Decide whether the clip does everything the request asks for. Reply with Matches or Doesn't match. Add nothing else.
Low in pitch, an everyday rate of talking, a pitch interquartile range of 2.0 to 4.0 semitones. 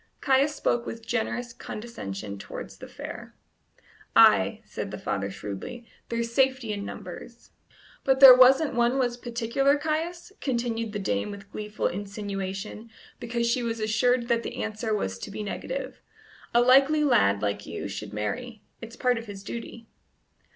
Doesn't match